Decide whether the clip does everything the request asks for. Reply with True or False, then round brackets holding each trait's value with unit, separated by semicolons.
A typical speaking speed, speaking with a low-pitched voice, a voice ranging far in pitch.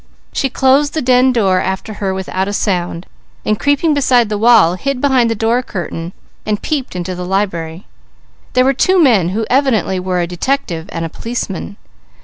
False (180 wpm; 215 Hz; 5.9 semitones)